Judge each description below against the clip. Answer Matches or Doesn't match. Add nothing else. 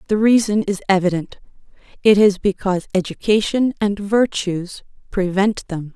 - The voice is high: Matches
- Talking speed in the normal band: Doesn't match